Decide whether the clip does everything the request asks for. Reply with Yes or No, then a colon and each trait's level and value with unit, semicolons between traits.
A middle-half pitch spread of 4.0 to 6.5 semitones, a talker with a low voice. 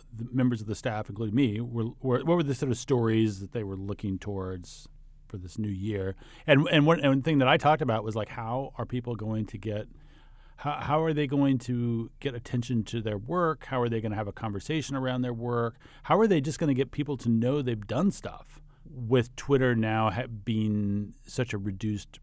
Yes: average, 4.3 semitones; low, 120 Hz